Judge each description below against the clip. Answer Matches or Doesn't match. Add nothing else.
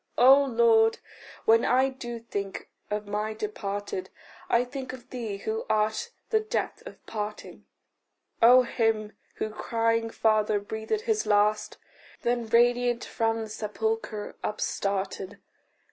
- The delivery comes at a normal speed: Doesn't match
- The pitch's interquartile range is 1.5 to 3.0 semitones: Matches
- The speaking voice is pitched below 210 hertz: Doesn't match